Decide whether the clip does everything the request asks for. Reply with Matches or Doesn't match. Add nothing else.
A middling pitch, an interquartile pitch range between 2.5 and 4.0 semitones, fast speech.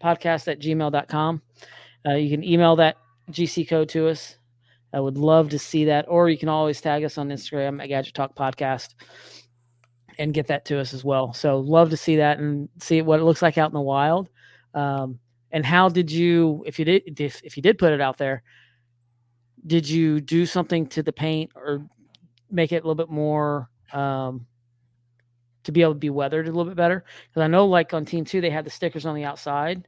Matches